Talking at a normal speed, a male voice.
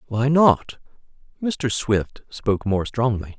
No: slow, 125 wpm; male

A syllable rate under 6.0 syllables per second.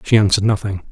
No: 7.5 syllables/s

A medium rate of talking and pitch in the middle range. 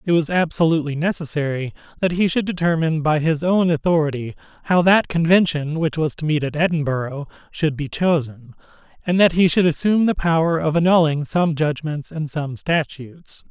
Yes: average, 170 wpm; medium, 160 Hz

